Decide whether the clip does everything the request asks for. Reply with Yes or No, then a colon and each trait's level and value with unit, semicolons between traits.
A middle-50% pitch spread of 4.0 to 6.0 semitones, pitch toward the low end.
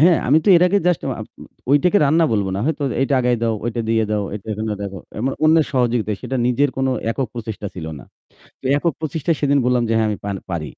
Yes: average, 5.3 semitones; low, 125 Hz